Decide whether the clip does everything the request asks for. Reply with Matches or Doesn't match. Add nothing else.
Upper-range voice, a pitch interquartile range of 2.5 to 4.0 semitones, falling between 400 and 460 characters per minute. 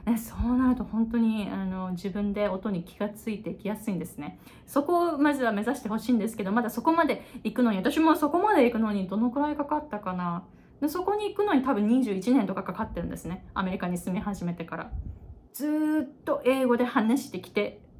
Doesn't match